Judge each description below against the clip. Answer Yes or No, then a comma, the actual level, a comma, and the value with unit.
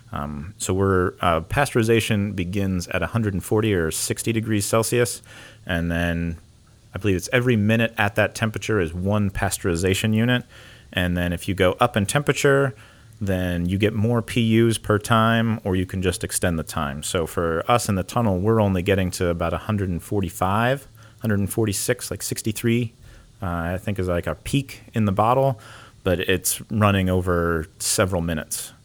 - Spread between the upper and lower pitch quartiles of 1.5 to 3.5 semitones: No, average, 3.9 semitones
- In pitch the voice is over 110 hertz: No, low, 105 Hz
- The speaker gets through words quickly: No, average, 185 wpm